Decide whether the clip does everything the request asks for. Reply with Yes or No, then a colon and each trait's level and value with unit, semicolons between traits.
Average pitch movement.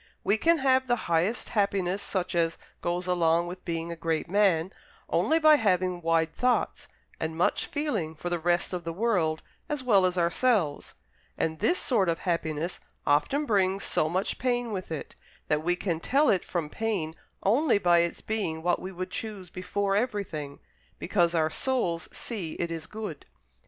Yes: average, 4.6 semitones